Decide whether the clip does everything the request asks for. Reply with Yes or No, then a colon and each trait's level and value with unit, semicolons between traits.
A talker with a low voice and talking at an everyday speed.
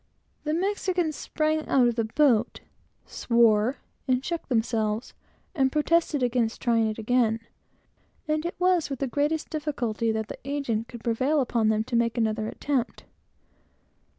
No: very high, 250 Hz; average, 150 wpm